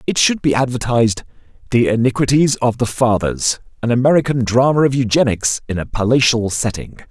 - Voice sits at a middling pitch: No, low, 120 Hz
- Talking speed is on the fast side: No, average, 150 wpm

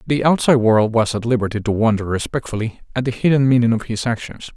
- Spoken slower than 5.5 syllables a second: No, 6.3 syllables/s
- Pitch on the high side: No, low, 115 Hz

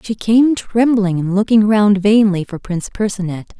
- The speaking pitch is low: No, high, 205 Hz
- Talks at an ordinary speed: Yes, average, 165 wpm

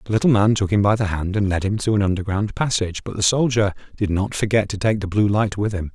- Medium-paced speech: No, fast, 285 wpm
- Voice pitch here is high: No, low, 100 Hz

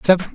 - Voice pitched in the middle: Yes, medium, 180 Hz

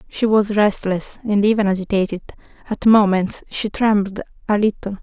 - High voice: Yes, high, 205 Hz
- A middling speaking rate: Yes, average, 145 wpm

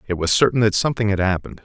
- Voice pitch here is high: No, low, 100 Hz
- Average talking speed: No, fast, 255 wpm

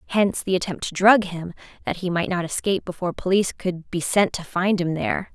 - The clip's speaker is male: No, female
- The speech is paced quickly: Yes, fast, 225 wpm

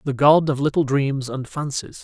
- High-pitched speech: No, medium, 140 Hz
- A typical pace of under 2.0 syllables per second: Yes, 1.5 syllables/s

